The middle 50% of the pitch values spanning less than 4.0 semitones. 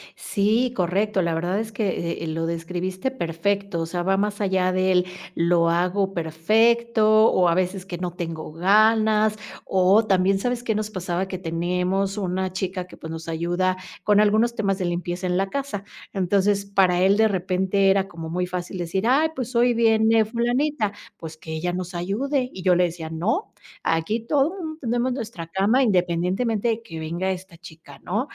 Yes: average, 3.6 semitones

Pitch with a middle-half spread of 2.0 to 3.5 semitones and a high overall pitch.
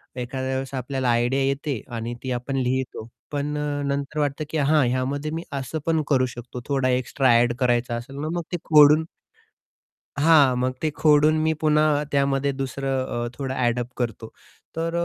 No: average, 2.8 semitones; low, 135 Hz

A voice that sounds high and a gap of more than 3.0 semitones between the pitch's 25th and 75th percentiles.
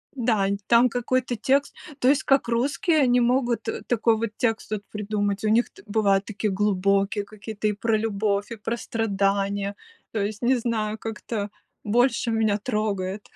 No: high, 220 Hz; average, 2.7 semitones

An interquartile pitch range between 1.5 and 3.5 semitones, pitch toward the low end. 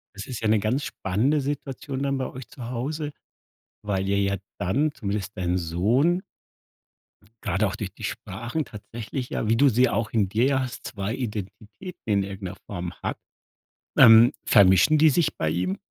No: average, 5.3 semitones; low, 110 Hz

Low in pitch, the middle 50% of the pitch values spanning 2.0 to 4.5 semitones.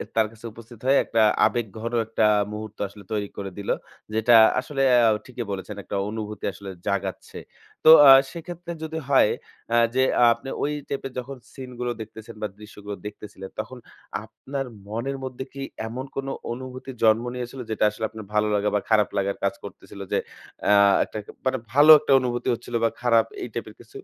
Yes: low, 115 Hz; average, 3.5 semitones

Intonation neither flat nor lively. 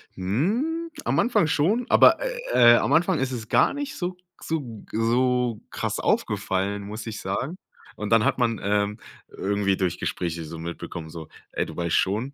No: wide, 8.0 semitones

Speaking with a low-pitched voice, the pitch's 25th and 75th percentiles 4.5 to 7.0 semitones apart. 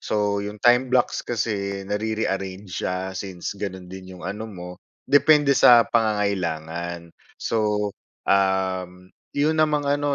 No: low, 100 Hz; average, 3.4 semitones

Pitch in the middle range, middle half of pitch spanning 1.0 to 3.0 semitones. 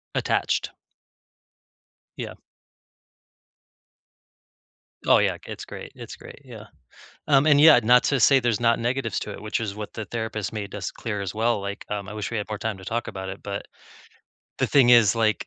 No: low, 110 Hz; narrow, 2.6 semitones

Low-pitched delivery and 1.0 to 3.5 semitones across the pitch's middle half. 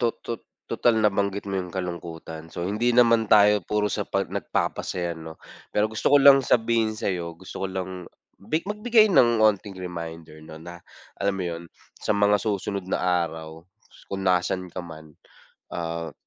No: very low, 95 Hz; average, 4.2 semitones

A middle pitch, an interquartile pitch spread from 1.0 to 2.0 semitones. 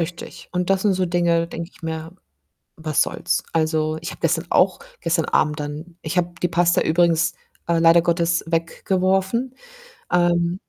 Yes: medium, 170 Hz; narrow, 1.5 semitones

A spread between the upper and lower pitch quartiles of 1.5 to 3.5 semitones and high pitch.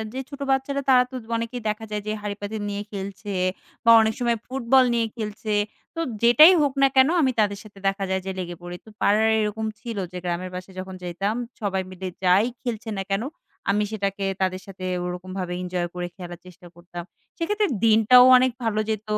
No: average, 4.0 semitones; high, 210 Hz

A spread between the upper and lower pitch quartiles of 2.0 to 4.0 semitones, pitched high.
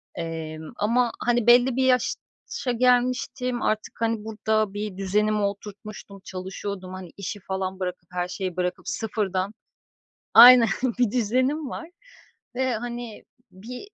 No: average, 4.4 semitones; high, 215 Hz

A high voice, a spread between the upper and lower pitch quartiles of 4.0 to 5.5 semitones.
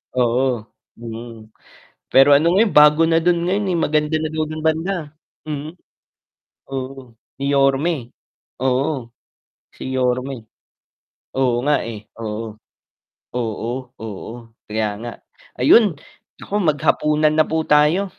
No: low, 135 Hz; average, 4.5 semitones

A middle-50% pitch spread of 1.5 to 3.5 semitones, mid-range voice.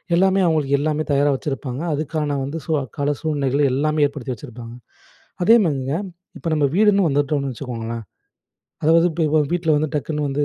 Yes: narrow, 2.4 semitones; medium, 145 Hz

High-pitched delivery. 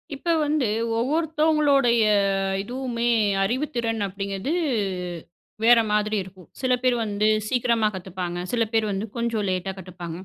Yes: high, 230 Hz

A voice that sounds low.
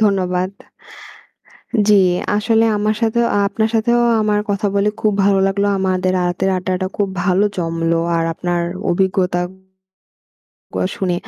No: high, 190 Hz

